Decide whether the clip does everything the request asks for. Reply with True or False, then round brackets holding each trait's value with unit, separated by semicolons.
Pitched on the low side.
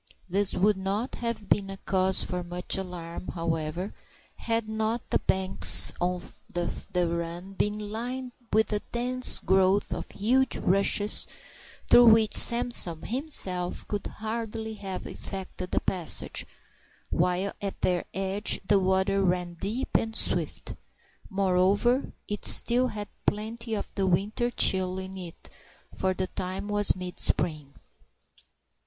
False (195 Hz)